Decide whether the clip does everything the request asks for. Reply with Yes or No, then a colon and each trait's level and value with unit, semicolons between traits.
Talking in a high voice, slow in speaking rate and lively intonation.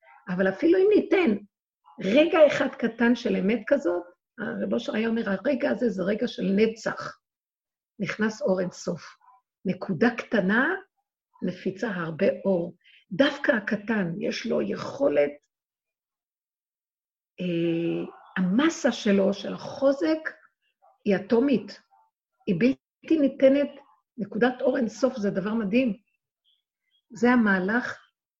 No: high, 230 Hz; average, 110 wpm; wide, 6.0 semitones